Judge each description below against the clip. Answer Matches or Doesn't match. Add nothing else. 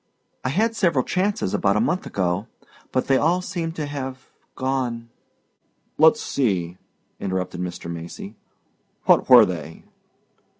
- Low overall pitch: Matches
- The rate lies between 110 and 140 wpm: Matches